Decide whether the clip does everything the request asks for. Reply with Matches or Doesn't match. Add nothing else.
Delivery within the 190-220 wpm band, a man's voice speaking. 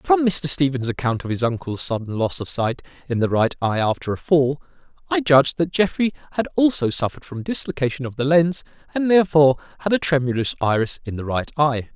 Matches